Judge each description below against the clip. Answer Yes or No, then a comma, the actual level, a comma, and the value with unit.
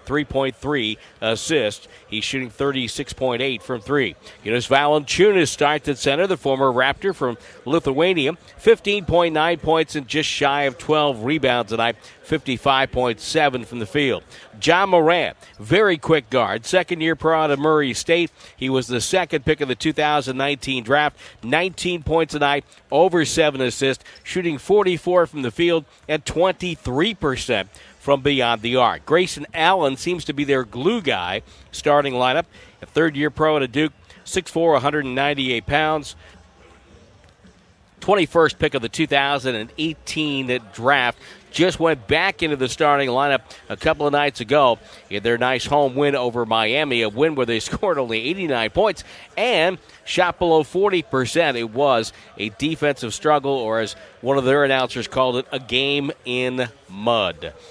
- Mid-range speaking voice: Yes, medium, 145 Hz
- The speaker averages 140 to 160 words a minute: Yes, average, 150 wpm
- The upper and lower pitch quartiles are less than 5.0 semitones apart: Yes, average, 3.9 semitones